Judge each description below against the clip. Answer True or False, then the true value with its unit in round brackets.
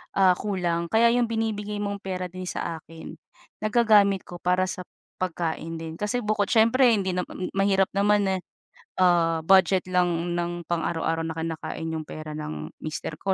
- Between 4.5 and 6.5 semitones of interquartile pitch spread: False (3.6 semitones)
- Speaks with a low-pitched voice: False (185 Hz)